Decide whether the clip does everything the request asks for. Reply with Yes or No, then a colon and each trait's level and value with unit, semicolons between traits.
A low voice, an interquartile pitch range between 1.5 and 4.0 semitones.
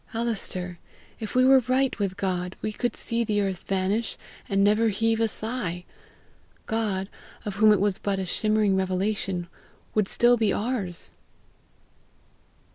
No: high, 205 Hz; average, 2.9 semitones